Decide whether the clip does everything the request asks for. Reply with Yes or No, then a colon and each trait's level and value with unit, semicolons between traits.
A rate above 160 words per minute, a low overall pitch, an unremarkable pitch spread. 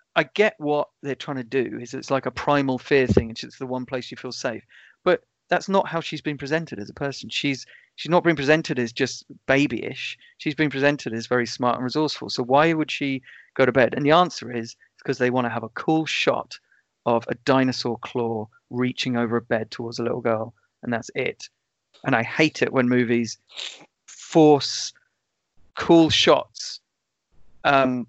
Yes: average, 195 wpm; low, 130 Hz; average, 3.9 semitones